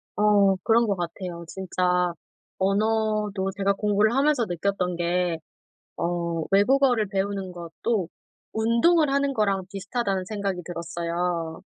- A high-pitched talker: Yes, high, 195 Hz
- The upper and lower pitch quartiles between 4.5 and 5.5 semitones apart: No, average, 3.6 semitones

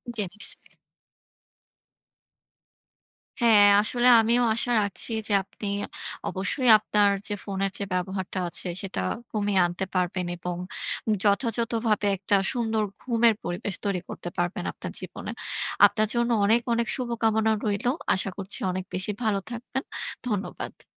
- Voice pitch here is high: Yes, high, 210 Hz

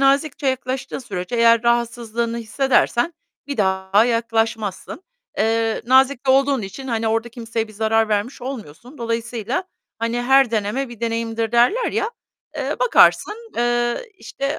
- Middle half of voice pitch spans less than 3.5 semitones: Yes, average, 2.9 semitones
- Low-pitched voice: No, high, 235 Hz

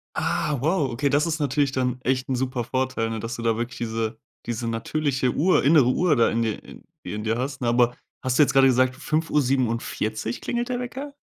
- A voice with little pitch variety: No, average, 3.8 semitones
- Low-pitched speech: Yes, low, 130 Hz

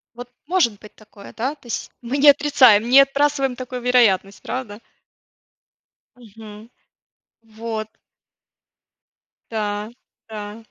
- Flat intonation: No, average, 3.6 semitones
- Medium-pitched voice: No, high, 230 Hz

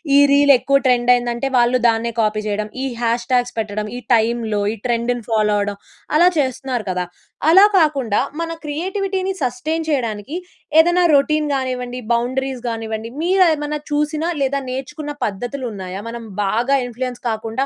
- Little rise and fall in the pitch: No, average, 4.4 semitones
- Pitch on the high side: Yes, very high, 250 Hz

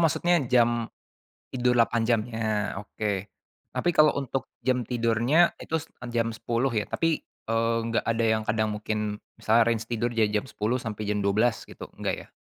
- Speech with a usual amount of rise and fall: No, narrow, 2.3 semitones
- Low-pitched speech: Yes, low, 115 Hz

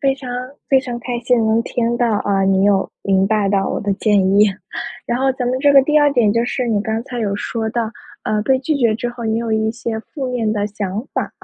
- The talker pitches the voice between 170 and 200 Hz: No, high, 230 Hz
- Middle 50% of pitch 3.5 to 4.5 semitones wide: No, average, 3.0 semitones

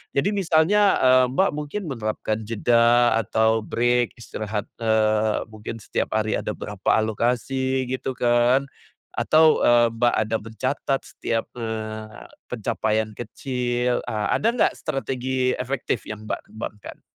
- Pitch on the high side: No, low, 120 Hz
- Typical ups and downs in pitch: Yes, average, 3.2 semitones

